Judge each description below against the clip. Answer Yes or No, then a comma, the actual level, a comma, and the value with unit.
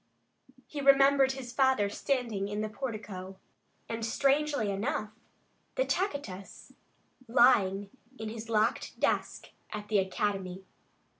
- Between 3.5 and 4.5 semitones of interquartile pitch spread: No, average, 5.0 semitones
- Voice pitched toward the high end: Yes, high, 220 Hz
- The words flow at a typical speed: No, slow, 115 wpm